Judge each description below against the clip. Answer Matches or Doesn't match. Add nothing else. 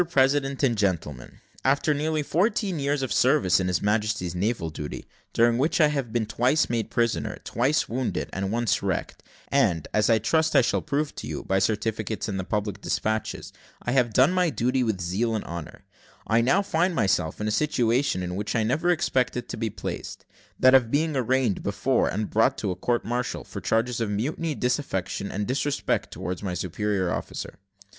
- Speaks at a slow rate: Doesn't match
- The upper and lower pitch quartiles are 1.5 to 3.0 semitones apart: Doesn't match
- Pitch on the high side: Doesn't match